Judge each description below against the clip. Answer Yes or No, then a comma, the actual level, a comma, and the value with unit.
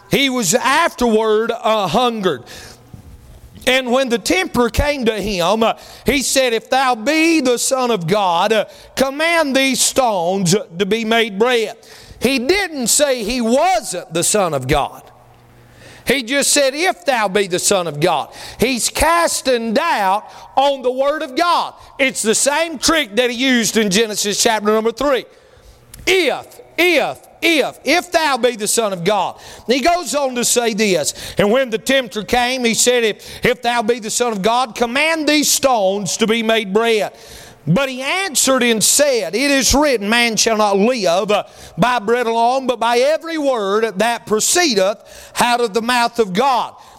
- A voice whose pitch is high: Yes, high, 240 Hz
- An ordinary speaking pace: Yes, average, 170 wpm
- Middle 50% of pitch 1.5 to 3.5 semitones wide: No, average, 3.9 semitones